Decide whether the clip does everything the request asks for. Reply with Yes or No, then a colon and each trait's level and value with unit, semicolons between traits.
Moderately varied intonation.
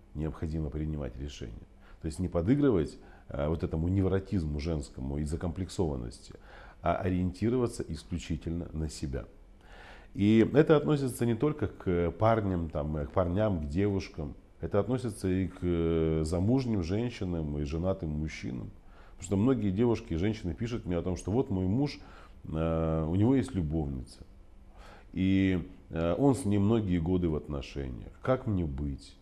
Yes: average, 4.5 semitones